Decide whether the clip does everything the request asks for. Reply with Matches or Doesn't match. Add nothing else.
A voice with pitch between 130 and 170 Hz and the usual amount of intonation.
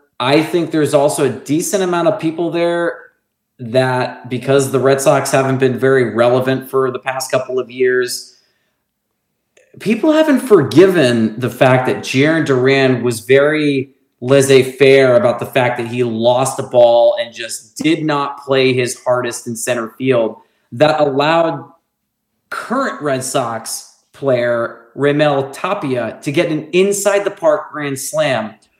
Matches